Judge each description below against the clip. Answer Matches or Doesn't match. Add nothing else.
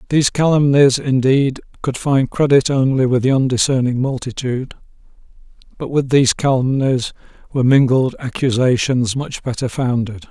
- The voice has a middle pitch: Doesn't match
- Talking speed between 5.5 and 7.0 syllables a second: Doesn't match